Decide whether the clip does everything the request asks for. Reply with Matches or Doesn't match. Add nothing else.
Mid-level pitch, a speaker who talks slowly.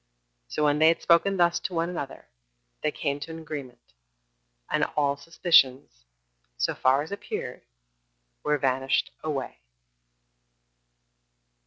Matches